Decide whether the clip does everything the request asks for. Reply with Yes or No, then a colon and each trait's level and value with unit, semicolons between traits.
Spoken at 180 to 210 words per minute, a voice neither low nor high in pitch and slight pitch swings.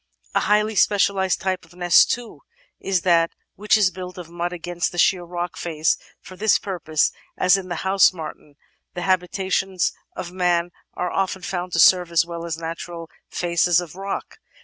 Yes: average, 190 wpm; medium, 180 Hz; narrow, 1.8 semitones